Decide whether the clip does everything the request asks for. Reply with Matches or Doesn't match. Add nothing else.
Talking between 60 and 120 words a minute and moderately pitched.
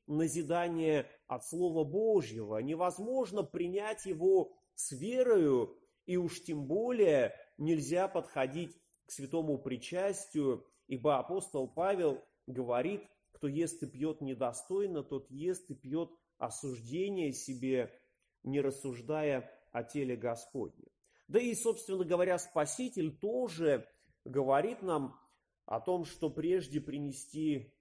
Matches